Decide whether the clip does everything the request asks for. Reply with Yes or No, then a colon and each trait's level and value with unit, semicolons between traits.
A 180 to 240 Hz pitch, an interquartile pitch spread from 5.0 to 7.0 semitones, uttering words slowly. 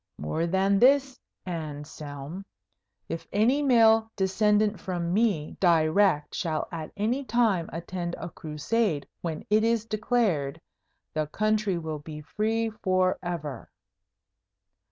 Yes: medium, 185 Hz; wide, 5.5 semitones; slow, 115 wpm